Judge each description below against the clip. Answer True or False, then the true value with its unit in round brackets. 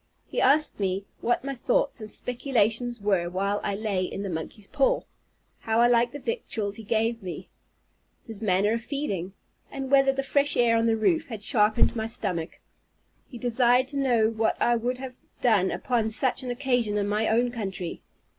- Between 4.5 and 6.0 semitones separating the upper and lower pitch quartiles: False (3.5 semitones)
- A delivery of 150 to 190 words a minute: True (185 wpm)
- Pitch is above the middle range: True (230 Hz)